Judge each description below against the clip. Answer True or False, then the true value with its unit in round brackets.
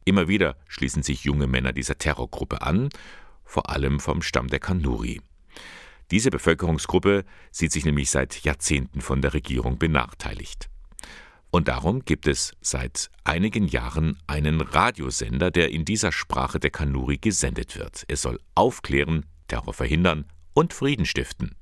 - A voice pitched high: False (75 Hz)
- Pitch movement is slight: False (3.5 semitones)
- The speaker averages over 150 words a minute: False (140 wpm)